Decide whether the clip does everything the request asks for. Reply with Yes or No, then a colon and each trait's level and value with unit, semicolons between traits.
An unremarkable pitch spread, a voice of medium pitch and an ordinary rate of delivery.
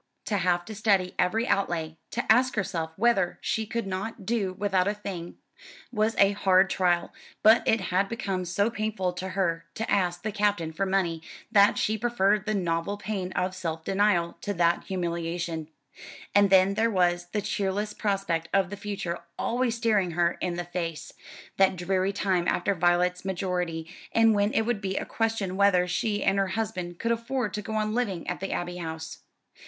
No: average, 3.0 semitones; high, 195 Hz; average, 180 wpm